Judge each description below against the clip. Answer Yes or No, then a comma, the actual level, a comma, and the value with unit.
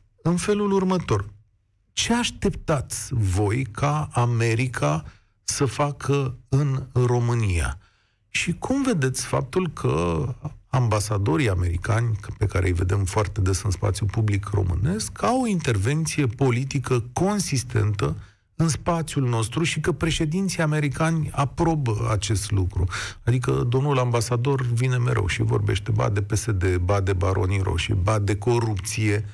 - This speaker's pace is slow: No, average, 125 wpm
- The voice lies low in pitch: Yes, low, 120 Hz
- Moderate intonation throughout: No, wide, 5.7 semitones